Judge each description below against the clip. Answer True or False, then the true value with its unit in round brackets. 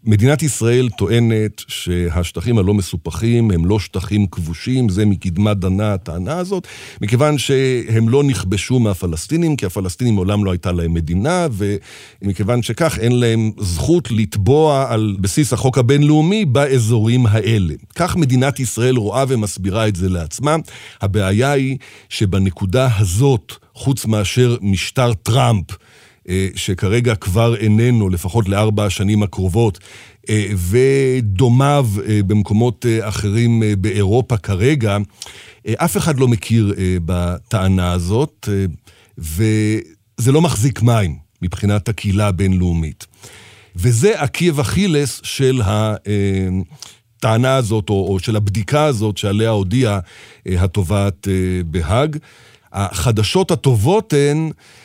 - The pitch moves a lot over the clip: False (4.2 semitones)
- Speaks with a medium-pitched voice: False (110 Hz)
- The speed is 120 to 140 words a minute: False (105 wpm)